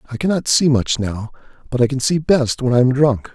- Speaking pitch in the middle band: No, low, 130 Hz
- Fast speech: Yes, fast, 250 wpm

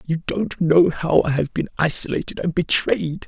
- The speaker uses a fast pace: No, average, 185 wpm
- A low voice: No, medium, 165 Hz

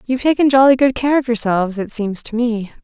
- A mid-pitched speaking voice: No, high, 240 Hz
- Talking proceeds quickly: Yes, fast, 235 wpm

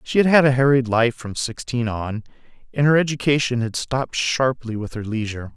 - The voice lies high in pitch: No, low, 125 Hz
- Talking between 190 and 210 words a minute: Yes, average, 195 wpm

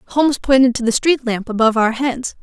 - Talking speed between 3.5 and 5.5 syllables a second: No, 5.9 syllables/s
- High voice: Yes, very high, 250 Hz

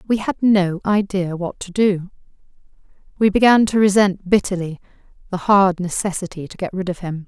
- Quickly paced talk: No, average, 165 wpm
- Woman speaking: Yes, female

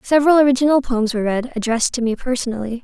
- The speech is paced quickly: No, average, 190 wpm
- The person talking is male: No, female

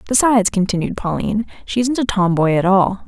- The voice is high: Yes, high, 205 Hz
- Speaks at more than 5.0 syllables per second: Yes, 5.9 syllables/s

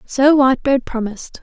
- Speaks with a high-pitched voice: Yes, very high, 260 Hz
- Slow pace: Yes, slow, 125 wpm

